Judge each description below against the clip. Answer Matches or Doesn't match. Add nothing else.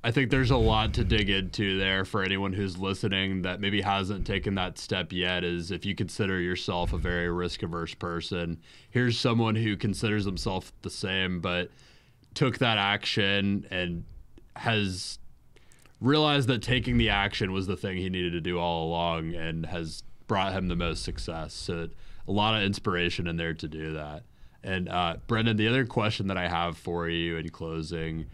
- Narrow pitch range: Doesn't match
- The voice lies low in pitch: Matches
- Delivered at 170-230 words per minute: Matches